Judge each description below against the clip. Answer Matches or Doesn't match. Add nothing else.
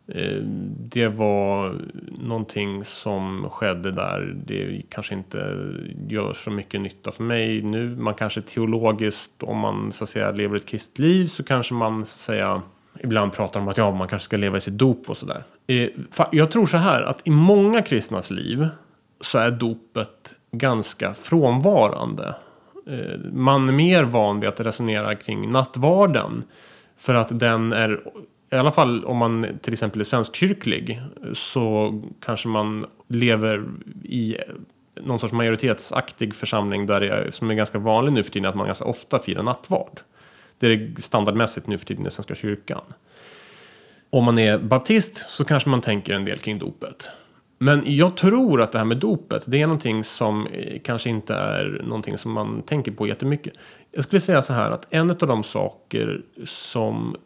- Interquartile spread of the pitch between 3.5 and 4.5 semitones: Matches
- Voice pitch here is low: Matches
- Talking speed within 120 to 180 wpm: Matches